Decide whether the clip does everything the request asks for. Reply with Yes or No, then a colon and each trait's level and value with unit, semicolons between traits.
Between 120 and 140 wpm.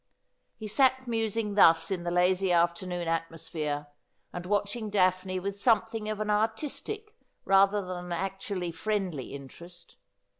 Yes: slow, 135 wpm